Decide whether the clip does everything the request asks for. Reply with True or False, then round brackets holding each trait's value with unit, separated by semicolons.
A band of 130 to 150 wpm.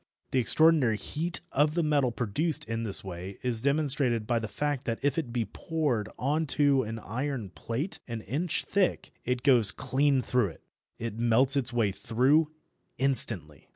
False (170 wpm)